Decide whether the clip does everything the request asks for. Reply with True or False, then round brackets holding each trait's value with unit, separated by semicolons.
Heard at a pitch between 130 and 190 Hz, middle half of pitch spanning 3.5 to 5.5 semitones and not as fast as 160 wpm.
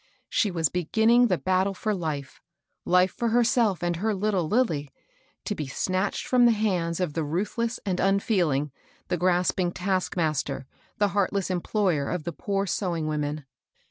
False (185 Hz; 3.9 semitones; 165 wpm)